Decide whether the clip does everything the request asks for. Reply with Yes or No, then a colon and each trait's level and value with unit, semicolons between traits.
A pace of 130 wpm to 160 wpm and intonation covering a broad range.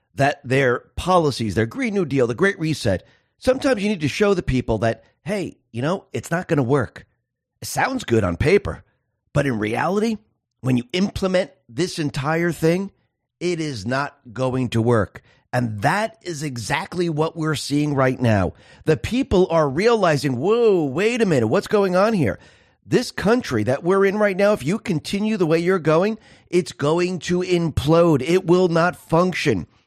No: average, 175 wpm; wide, 6.6 semitones